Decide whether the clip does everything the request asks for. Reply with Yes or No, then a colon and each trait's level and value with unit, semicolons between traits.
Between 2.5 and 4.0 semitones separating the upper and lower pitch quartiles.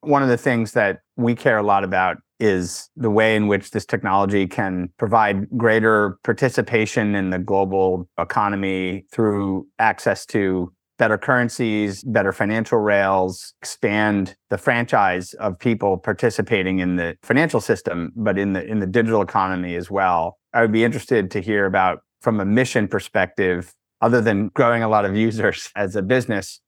Yes: average, 3.2 semitones